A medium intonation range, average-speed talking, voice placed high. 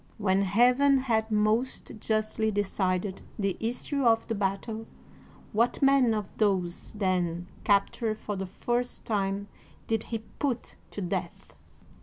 No: average, 3.0 semitones; slow, 130 wpm; high, 215 Hz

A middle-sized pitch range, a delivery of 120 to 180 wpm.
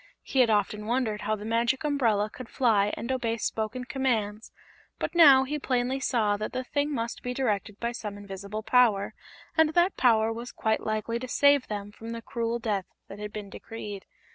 No: average, 3.3 semitones; average, 190 wpm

